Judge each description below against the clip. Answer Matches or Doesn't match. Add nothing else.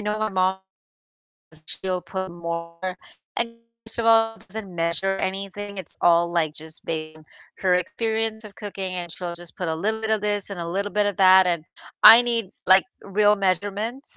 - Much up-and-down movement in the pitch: Doesn't match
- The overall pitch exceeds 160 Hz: Matches